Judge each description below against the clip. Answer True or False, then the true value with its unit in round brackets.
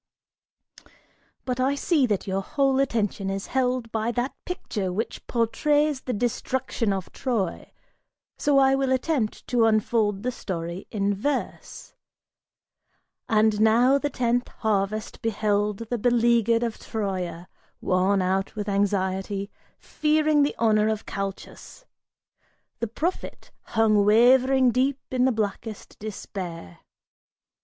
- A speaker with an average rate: False (120 wpm)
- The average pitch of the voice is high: True (225 Hz)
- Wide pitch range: False (4.2 semitones)